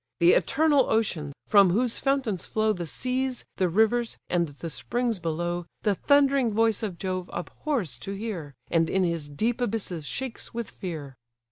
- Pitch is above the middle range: Yes, high, 200 Hz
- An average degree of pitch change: No, wide, 5.8 semitones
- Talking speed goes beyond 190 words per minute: No, average, 160 wpm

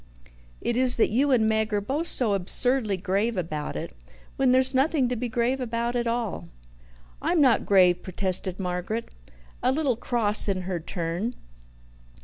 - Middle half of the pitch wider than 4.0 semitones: Yes, average, 4.9 semitones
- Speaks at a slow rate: No, average, 160 wpm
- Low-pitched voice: No, high, 230 Hz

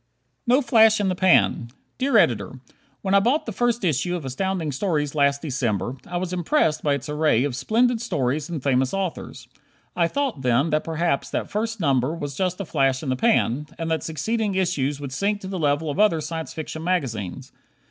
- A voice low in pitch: No, medium, 160 Hz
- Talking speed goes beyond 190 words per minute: Yes, average, 200 wpm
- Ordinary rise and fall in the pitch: No, wide, 5.8 semitones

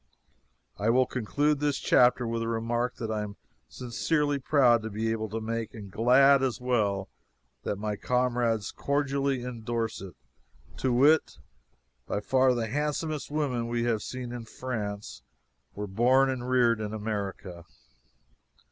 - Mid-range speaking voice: No, low, 120 Hz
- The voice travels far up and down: No, average, 3.0 semitones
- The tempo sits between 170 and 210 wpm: No, average, 150 wpm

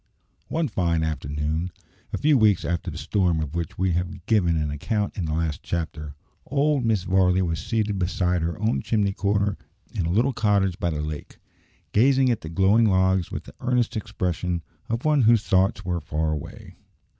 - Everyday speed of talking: Yes, average, 185 wpm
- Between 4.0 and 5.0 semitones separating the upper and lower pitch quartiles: Yes, average, 4.7 semitones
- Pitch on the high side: No, very low, 95 Hz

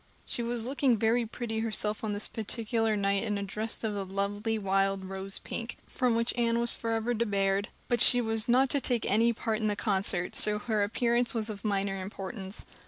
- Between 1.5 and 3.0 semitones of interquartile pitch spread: Yes, average, 2.7 semitones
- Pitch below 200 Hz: No, high, 220 Hz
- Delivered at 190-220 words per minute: Yes, average, 200 wpm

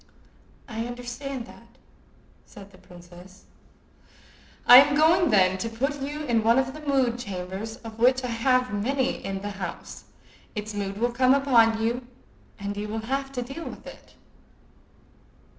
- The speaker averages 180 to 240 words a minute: No, average, 160 wpm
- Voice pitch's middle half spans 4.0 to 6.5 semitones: Yes, average, 4.4 semitones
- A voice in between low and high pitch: No, high, 235 Hz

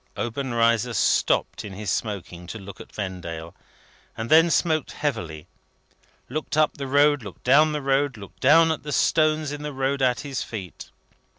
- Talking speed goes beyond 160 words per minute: Yes, average, 170 wpm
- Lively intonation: Yes, wide, 6.3 semitones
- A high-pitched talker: No, low, 130 Hz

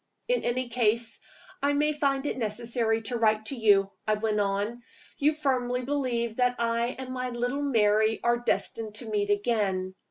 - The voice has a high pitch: Yes, high, 235 Hz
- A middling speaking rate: Yes, average, 170 wpm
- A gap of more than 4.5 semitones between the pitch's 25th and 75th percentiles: No, average, 2.9 semitones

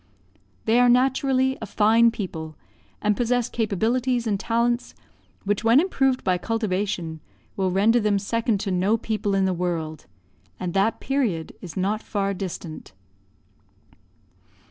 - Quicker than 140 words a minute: No, slow, 135 wpm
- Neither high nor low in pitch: No, high, 210 Hz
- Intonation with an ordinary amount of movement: Yes, average, 4.0 semitones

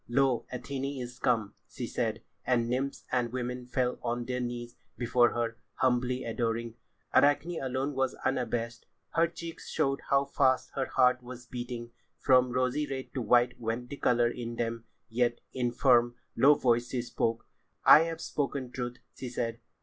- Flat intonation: Yes, narrow, 1.7 semitones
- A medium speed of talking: Yes, average, 165 wpm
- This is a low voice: Yes, low, 125 Hz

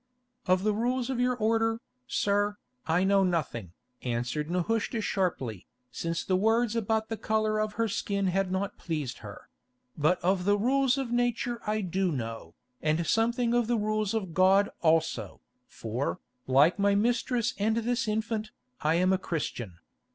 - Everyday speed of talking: Yes, average, 160 wpm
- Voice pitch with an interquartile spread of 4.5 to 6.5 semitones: Yes, average, 5.1 semitones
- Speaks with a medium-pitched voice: No, high, 200 Hz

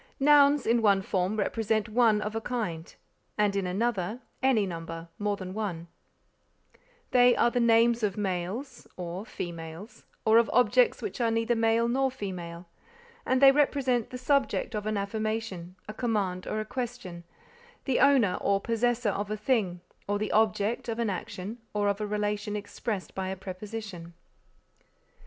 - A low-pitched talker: No, high, 215 Hz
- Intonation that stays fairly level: No, average, 3.7 semitones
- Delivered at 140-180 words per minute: Yes, average, 160 wpm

